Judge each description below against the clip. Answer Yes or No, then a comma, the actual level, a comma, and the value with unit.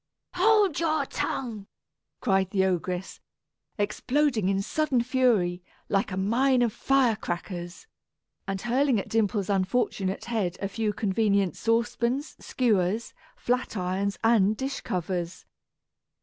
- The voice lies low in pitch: No, high, 215 Hz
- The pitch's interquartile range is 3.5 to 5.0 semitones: Yes, average, 4.7 semitones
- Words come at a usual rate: No, slow, 120 wpm